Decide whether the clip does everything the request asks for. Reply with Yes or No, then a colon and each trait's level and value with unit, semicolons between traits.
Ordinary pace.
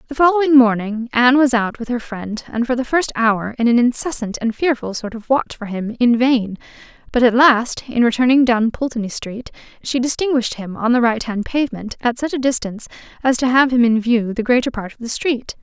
No: fast, 225 wpm